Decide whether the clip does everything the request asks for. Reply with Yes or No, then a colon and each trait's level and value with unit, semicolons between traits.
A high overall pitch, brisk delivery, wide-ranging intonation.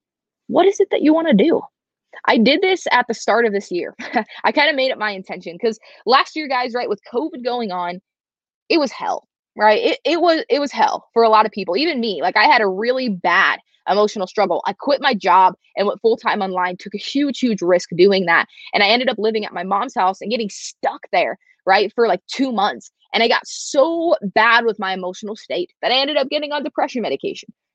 Yes: high, 230 Hz; fast, 235 wpm; wide, 6.0 semitones